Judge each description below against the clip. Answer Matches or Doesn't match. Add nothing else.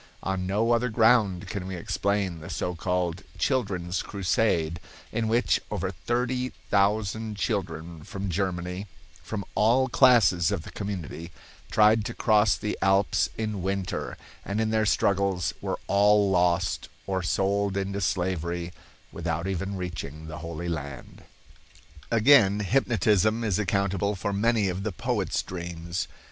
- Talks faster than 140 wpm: Doesn't match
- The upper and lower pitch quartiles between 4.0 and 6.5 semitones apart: Doesn't match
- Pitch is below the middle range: Matches